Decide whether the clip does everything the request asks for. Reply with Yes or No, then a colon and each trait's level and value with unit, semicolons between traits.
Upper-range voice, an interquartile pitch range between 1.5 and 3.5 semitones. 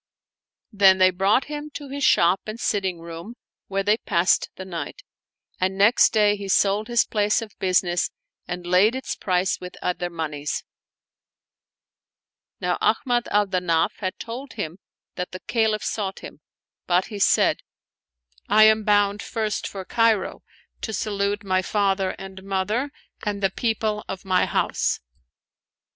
Yes: high, 195 Hz; average, 2.8 semitones